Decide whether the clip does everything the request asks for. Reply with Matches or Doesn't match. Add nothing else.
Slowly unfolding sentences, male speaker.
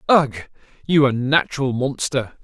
Matches